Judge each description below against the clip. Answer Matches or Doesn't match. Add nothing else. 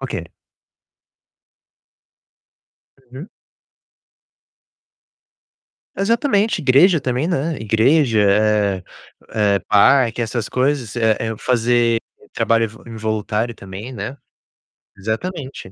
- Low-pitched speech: Matches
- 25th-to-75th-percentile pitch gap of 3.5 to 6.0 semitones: Matches